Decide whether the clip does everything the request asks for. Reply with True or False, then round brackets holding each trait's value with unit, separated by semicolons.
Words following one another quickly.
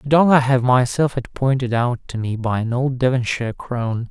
True (220 wpm)